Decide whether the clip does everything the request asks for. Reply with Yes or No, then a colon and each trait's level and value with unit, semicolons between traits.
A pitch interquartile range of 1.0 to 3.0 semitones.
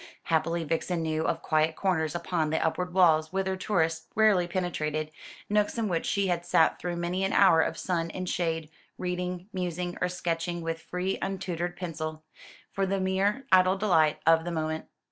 Yes: narrow, 2.4 semitones